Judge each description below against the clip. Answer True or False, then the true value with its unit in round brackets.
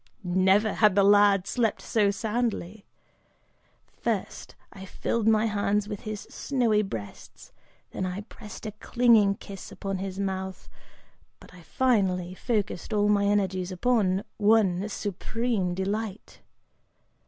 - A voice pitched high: True (205 Hz)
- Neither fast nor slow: False (125 wpm)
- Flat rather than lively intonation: True (2.3 semitones)